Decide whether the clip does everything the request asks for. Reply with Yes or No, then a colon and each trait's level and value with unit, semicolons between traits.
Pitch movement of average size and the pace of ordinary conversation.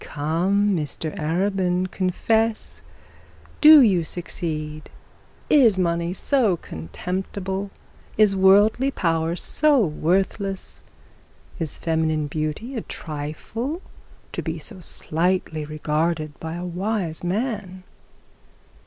No: average, 4.2 semitones; slow, 95 wpm